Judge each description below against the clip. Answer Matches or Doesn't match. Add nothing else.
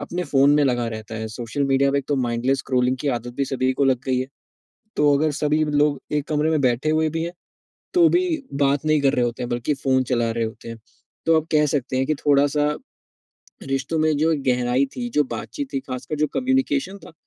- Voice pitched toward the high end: Doesn't match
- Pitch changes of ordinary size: Matches